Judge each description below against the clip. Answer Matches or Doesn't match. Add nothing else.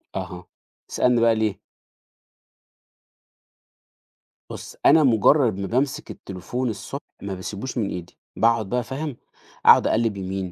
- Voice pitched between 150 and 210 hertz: Doesn't match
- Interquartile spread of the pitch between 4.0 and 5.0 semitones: Matches